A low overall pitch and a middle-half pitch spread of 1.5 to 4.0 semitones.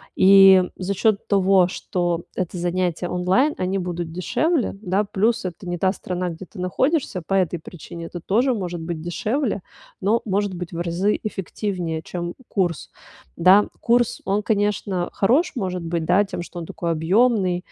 No: medium, 185 Hz; average, 2.8 semitones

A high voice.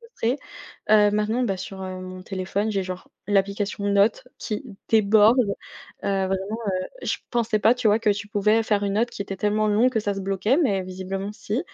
Yes: high, 205 Hz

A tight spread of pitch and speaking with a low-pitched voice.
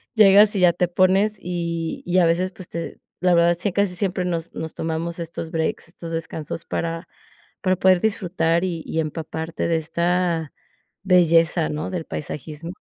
No: narrow, 2.0 semitones; medium, 170 Hz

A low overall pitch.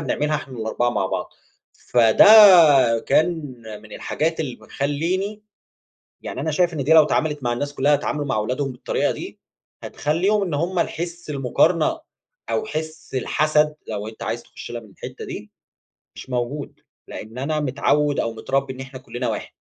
No: medium, 145 Hz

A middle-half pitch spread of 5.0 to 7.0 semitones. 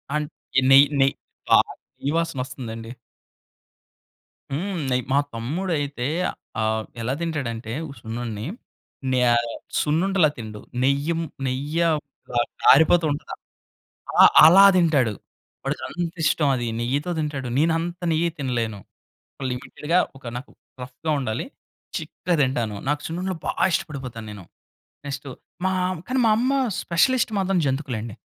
Yes: wide, 5.4 semitones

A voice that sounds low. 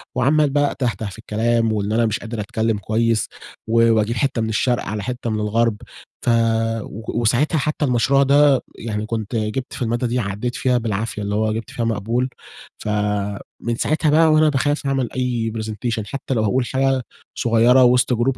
Yes: low, 115 Hz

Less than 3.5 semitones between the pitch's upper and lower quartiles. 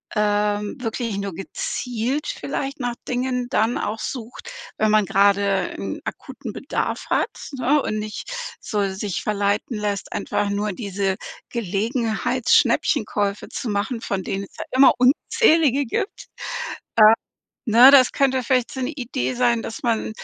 No: average, 3.8 semitones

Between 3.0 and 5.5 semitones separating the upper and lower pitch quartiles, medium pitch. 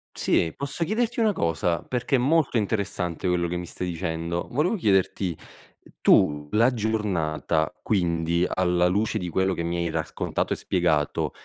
No: average, 4.8 semitones; very low, 90 Hz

